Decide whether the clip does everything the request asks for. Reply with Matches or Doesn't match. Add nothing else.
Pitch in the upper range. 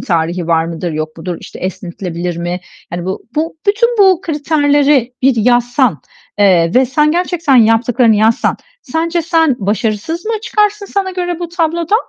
Matches